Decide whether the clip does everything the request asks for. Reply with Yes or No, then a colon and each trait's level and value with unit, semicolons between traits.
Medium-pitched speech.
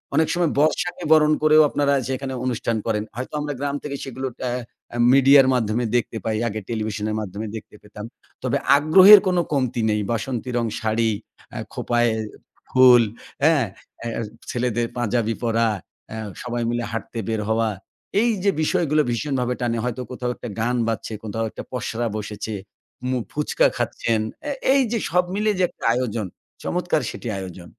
No: low, 120 Hz